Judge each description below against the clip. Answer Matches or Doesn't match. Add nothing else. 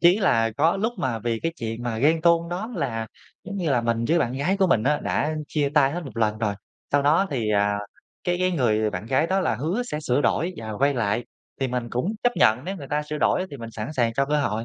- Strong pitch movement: Matches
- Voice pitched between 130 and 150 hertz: Matches